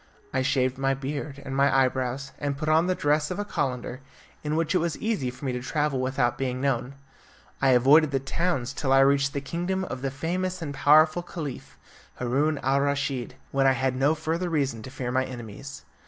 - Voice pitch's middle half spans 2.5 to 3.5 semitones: Yes, average, 2.9 semitones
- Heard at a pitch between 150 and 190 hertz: No, medium, 140 Hz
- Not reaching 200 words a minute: No, fast, 205 wpm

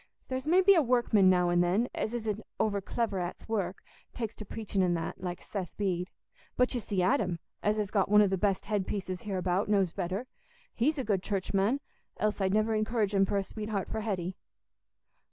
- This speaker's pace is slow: No, average, 195 wpm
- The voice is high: Yes, high, 205 Hz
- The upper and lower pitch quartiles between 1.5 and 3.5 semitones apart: Yes, average, 2.8 semitones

